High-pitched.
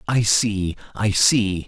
No: low, 105 Hz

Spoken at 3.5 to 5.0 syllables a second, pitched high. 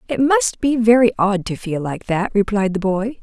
Yes: 4.7 syllables/s; high, 215 Hz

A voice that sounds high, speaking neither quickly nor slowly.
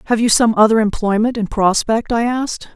Yes: high, 220 Hz; average, 195 wpm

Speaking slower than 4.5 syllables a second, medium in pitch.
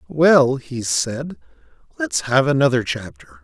Yes: 4.0 syllables/s; medium, 145 Hz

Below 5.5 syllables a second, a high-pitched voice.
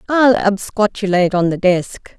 Yes: 4.6 syllables/s; high, 200 Hz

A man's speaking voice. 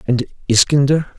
Yes: male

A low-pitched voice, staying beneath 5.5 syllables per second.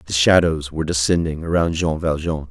Yes: very low, 80 Hz; 5.3 syllables/s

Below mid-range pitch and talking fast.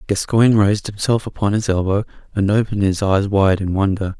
No: low, 100 Hz; average, 185 wpm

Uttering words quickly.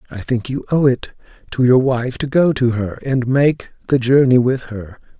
Yes: fast, 210 wpm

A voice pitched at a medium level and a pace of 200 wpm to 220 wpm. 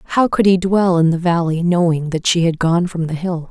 No: medium, 170 Hz; fast, 255 wpm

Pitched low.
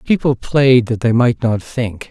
Yes: low, 120 Hz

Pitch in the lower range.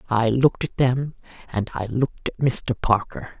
Yes: low, 120 Hz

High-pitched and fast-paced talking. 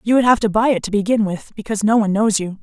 Yes: high, 210 Hz; fast, 320 wpm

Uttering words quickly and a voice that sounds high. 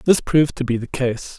No: fast, 260 wpm; low, 130 Hz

